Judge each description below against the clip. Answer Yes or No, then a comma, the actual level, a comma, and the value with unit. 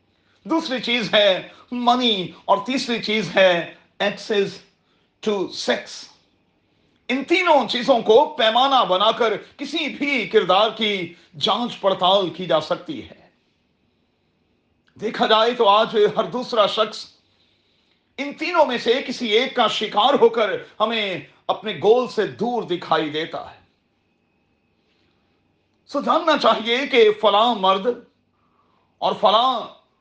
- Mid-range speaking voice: No, high, 220 Hz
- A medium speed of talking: Yes, average, 125 wpm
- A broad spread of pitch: No, average, 4.2 semitones